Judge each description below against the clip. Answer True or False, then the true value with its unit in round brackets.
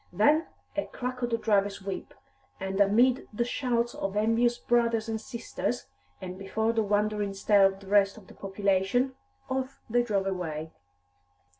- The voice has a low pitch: False (215 Hz)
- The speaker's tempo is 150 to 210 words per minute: True (160 wpm)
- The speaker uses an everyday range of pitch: True (3.4 semitones)